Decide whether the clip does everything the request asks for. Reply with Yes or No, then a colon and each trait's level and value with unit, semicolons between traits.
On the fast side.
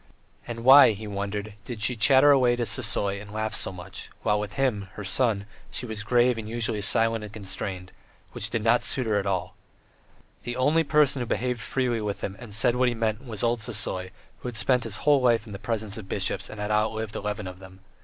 Yes: fast, 225 wpm